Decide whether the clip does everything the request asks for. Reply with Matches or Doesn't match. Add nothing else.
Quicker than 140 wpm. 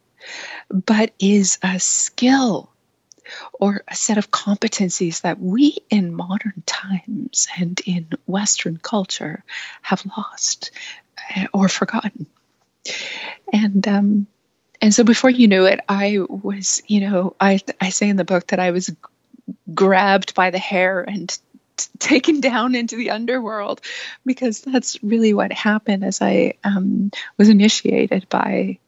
Doesn't match